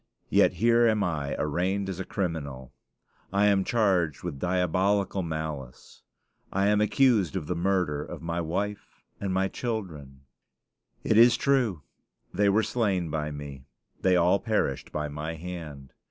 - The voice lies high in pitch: No, very low, 90 Hz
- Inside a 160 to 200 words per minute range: No, average, 150 wpm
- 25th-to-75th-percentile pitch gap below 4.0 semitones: No, average, 4.9 semitones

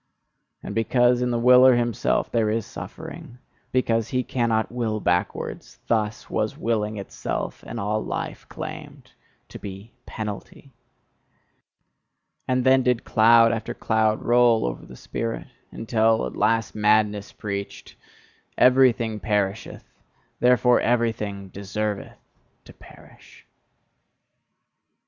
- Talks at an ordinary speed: No, slow, 110 wpm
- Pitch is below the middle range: Yes, low, 115 Hz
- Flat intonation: Yes, narrow, 2.3 semitones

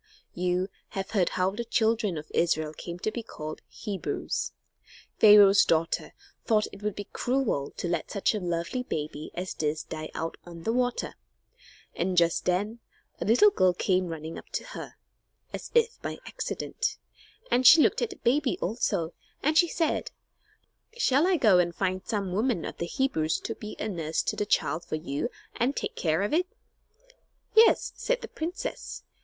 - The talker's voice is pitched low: No, high, 195 Hz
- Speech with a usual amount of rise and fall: No, wide, 6.4 semitones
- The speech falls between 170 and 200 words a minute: Yes, average, 180 wpm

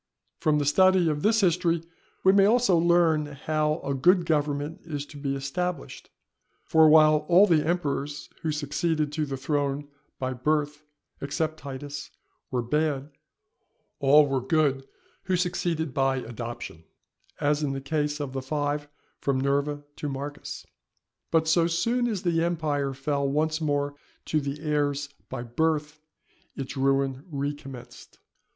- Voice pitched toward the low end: No, medium, 150 Hz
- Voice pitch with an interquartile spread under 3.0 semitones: Yes, narrow, 2.6 semitones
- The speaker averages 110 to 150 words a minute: Yes, average, 145 wpm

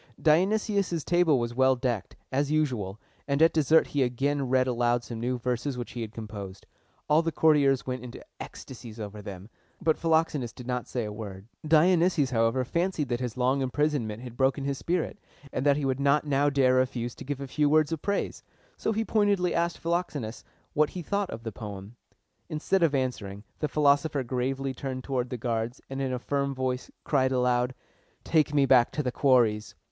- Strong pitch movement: No, average, 3.8 semitones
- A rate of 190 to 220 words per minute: Yes, average, 195 wpm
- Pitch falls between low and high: No, low, 130 Hz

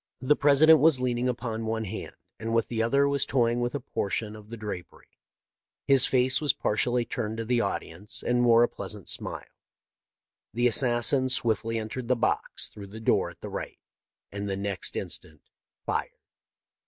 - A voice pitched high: No, low, 115 Hz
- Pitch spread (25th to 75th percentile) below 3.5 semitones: Yes, average, 2.7 semitones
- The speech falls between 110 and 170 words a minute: No, average, 180 wpm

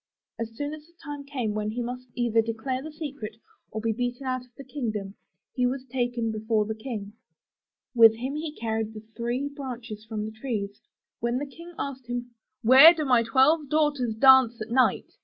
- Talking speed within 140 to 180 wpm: No, average, 195 wpm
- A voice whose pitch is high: Yes, high, 245 Hz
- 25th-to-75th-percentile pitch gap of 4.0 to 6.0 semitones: No, average, 3.5 semitones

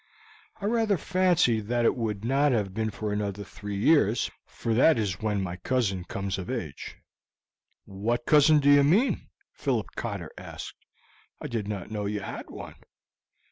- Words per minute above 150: Yes, average, 165 wpm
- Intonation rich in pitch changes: Yes, wide, 6.0 semitones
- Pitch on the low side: Yes, low, 110 Hz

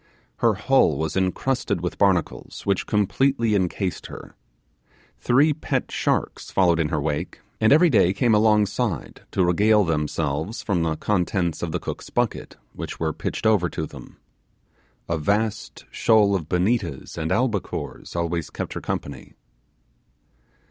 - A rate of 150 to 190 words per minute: No, average, 140 wpm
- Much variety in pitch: No, average, 4.9 semitones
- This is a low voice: Yes, very low, 95 Hz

